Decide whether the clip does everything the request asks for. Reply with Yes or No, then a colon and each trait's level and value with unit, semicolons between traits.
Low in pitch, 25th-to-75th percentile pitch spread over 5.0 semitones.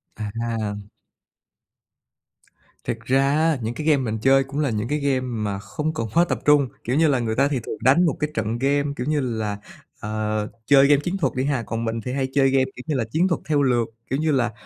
No: low, 130 Hz; average, 4.2 semitones